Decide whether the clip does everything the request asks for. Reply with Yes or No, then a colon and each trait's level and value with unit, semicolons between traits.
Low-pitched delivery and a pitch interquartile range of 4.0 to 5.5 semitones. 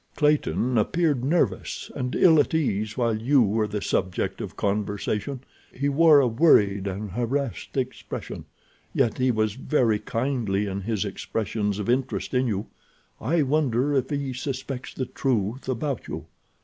Yes: low, 125 Hz; average, 4.7 semitones